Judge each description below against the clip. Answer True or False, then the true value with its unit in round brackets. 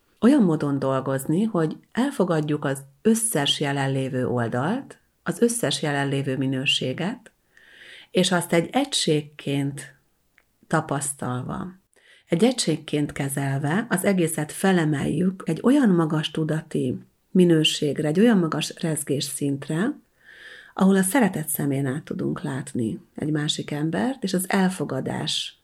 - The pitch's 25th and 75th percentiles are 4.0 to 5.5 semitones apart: True (5.2 semitones)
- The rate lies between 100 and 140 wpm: True (110 wpm)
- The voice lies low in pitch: False (155 Hz)